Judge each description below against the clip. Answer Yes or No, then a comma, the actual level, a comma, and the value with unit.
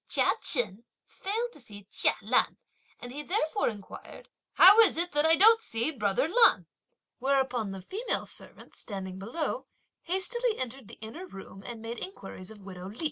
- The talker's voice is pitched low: No, very high, 260 Hz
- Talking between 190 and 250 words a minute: No, average, 165 wpm